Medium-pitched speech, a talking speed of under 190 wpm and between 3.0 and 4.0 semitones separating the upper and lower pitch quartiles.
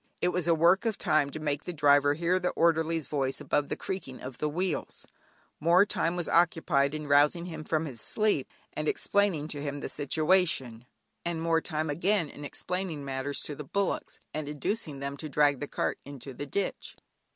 No: medium, 155 Hz; average, 195 wpm; average, 3.3 semitones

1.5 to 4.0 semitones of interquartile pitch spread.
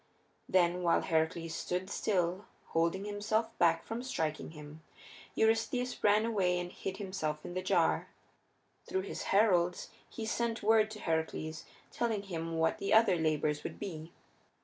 No: average, 4.6 semitones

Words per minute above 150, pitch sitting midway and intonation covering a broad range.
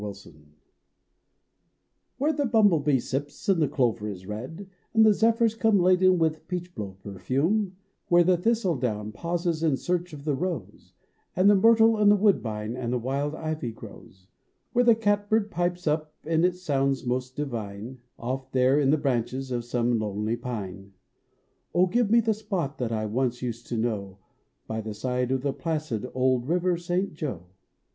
Yes: average, 165 wpm; medium, 145 Hz; wide, 7.3 semitones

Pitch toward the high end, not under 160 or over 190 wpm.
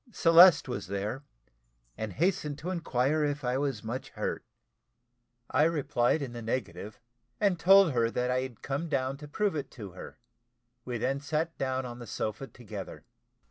No: low, 135 Hz; average, 170 wpm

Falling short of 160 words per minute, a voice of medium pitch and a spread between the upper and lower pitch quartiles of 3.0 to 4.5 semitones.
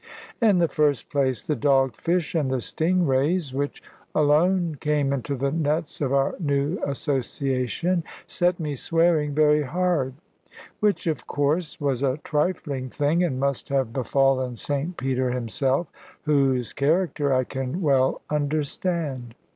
Yes: average, 140 wpm; medium, 145 Hz; average, 3.5 semitones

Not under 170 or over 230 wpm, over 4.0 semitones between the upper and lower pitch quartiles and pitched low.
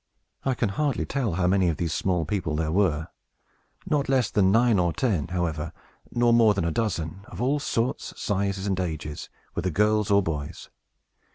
Yes: average, 180 wpm; wide, 5.4 semitones; very low, 95 Hz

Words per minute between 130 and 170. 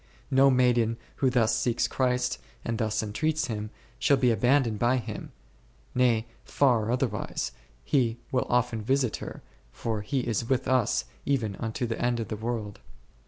Yes: average, 160 wpm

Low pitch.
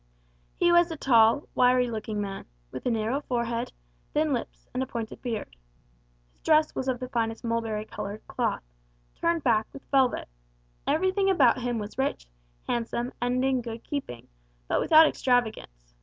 No: high, 245 Hz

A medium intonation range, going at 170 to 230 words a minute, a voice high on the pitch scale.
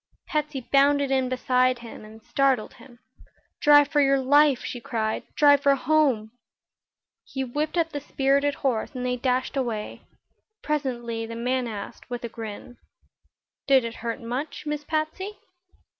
No: average, 3.4 semitones; average, 150 wpm; very high, 265 Hz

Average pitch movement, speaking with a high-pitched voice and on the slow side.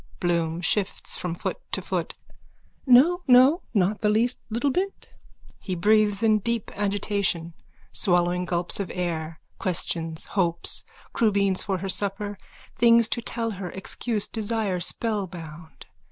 Yes: average, 4.2 semitones; high, 200 Hz; slow, 130 wpm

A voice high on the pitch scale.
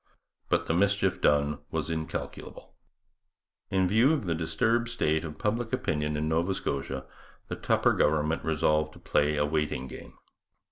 No: very low, 80 Hz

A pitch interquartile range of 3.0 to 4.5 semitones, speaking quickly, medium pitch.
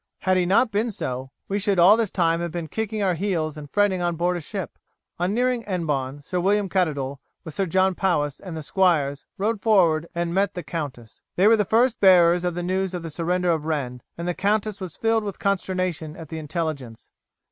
Yes: average, 3.8 semitones; fast, 215 wpm; medium, 180 Hz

